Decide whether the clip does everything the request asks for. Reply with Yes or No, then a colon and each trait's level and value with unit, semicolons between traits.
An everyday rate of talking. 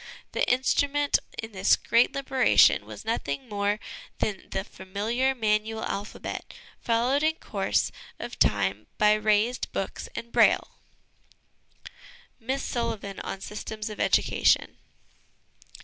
No: slow, 120 wpm